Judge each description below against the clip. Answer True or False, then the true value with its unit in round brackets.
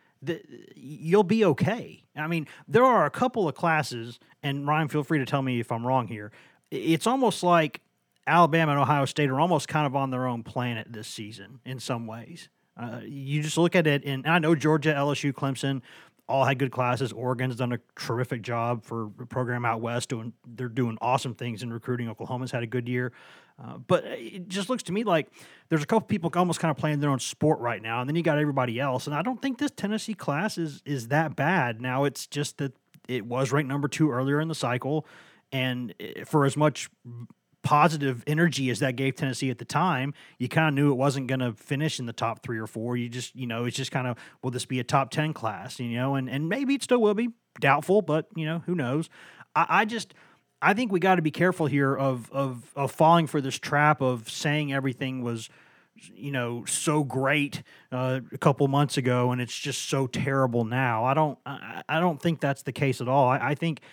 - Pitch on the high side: False (140 Hz)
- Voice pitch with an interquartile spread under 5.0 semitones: True (3.8 semitones)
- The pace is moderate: False (230 wpm)